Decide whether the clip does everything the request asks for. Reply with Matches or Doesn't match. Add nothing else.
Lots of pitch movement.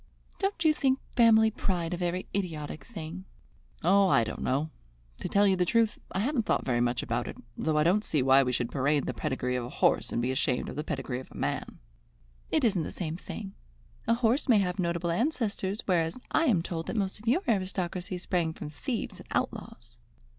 Matches